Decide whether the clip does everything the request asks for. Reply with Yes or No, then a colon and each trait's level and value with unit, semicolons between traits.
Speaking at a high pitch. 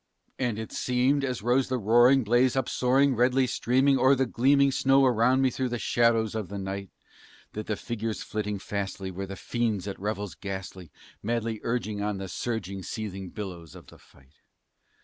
No: low, 115 Hz